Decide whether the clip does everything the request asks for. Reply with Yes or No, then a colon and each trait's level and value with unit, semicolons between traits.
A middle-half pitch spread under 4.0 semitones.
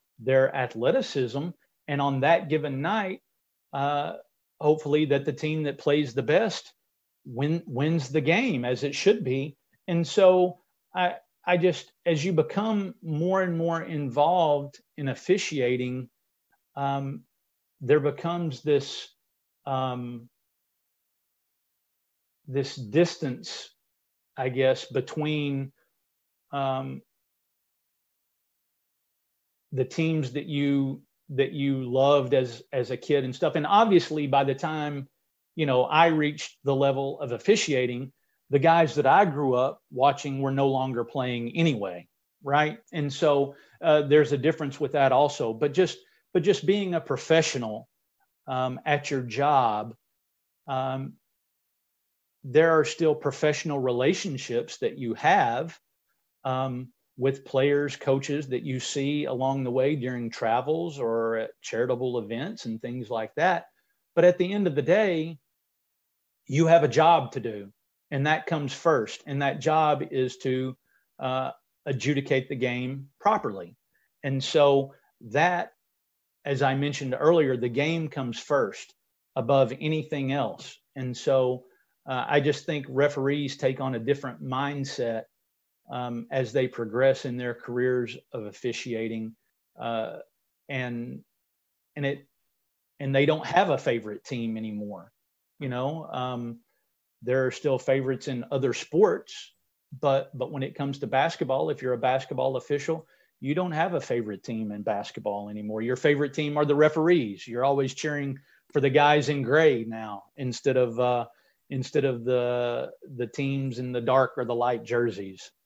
Yes: average, 3.1 semitones